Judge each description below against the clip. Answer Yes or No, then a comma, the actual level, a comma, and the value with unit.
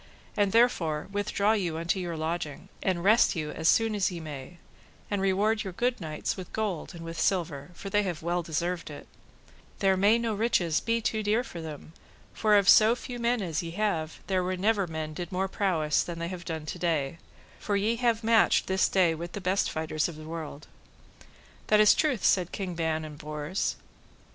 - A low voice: No, medium, 180 Hz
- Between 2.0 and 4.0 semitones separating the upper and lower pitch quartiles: No, average, 4.4 semitones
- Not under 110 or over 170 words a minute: No, average, 200 wpm